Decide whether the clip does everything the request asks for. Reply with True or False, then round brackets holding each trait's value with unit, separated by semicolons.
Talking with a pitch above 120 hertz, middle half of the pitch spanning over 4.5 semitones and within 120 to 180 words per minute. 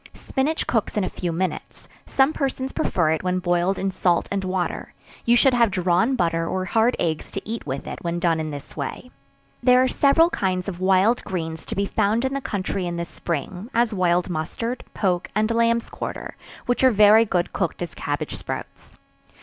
False (190 Hz; 5.1 semitones; 200 wpm)